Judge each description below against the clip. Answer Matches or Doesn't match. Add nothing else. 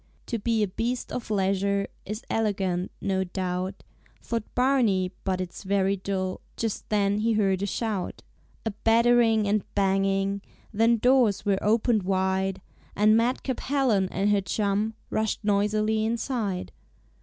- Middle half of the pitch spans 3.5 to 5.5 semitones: Doesn't match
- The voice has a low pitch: Doesn't match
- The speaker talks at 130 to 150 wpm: Matches